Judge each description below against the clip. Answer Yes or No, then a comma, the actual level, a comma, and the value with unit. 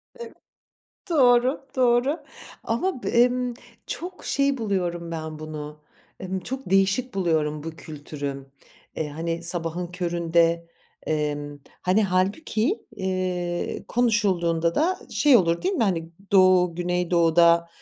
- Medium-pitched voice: Yes, medium, 180 Hz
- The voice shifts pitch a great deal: Yes, wide, 6.3 semitones